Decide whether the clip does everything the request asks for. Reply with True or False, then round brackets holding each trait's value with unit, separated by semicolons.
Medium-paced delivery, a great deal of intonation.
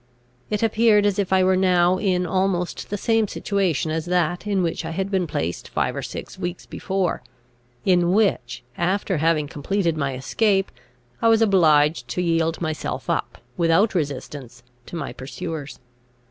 False (160 wpm; 3.6 semitones)